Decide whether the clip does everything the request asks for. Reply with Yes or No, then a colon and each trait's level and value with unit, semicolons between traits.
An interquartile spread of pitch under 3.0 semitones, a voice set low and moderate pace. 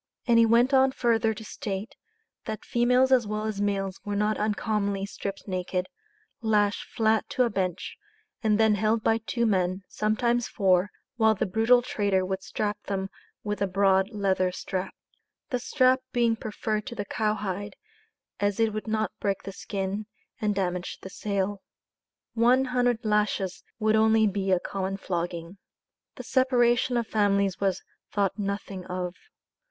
No: narrow, 2.6 semitones; high, 210 Hz; average, 160 wpm